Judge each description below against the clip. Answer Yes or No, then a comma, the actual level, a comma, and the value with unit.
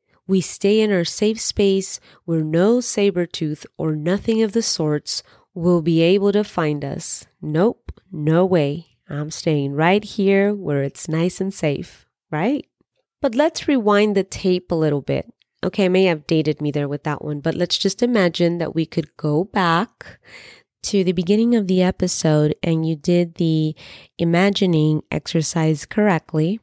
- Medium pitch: Yes, medium, 175 Hz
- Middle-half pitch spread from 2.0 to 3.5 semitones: No, average, 4.1 semitones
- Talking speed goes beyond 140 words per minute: Yes, average, 165 wpm